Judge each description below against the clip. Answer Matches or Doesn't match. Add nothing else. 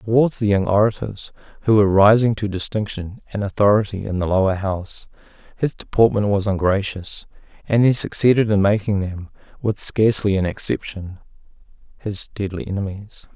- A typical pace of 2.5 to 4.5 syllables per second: Doesn't match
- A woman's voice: Doesn't match